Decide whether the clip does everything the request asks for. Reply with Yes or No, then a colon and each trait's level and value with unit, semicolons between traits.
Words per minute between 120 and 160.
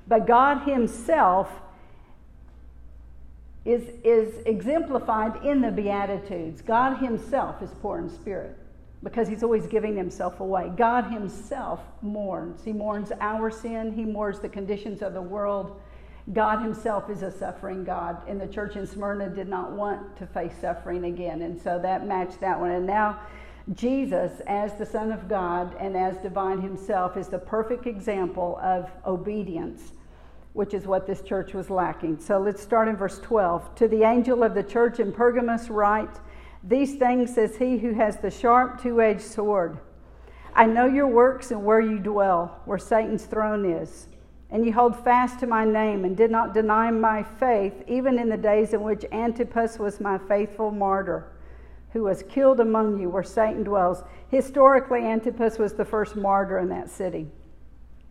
No: average, 170 wpm